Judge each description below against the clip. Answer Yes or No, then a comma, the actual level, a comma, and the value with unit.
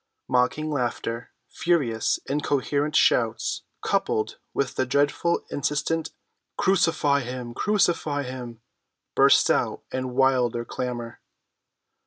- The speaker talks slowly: Yes, slow, 95 wpm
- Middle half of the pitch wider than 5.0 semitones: No, average, 3.6 semitones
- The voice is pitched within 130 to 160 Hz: Yes, low, 135 Hz